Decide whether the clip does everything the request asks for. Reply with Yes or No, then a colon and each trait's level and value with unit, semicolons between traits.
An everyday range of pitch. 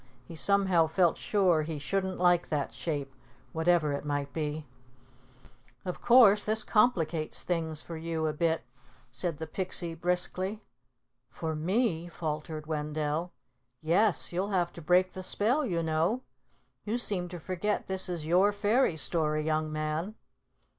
Yes: average, 3.4 semitones